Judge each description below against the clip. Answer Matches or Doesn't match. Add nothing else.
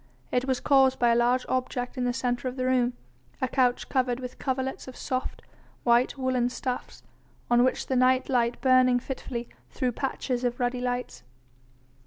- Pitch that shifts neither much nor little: Doesn't match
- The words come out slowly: Doesn't match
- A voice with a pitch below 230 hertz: Doesn't match